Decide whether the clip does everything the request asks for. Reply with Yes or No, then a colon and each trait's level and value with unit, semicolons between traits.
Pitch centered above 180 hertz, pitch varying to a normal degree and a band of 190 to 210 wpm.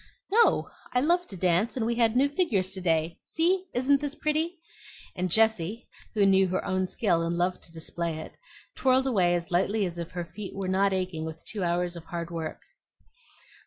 No: high, 190 Hz; wide, 6.0 semitones; average, 200 wpm